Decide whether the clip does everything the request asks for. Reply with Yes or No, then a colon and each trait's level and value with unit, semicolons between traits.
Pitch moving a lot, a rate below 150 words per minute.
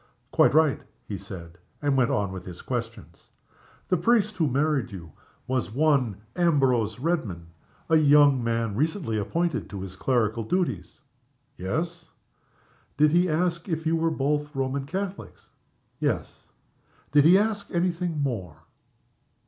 Yes: wide, 7.2 semitones; average, 140 wpm